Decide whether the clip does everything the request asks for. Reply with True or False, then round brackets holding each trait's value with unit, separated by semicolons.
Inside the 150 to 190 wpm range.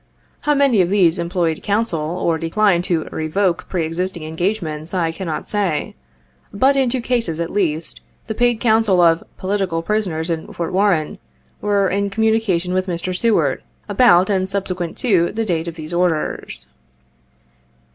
True (155 wpm)